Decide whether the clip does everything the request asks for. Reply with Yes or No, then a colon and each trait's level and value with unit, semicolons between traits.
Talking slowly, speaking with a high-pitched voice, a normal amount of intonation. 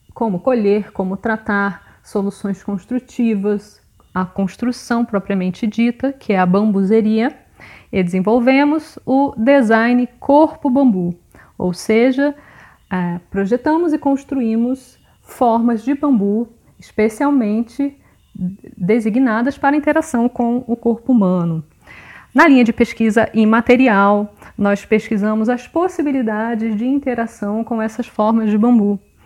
Yes: slow, 105 wpm; high, 230 Hz; average, 3.8 semitones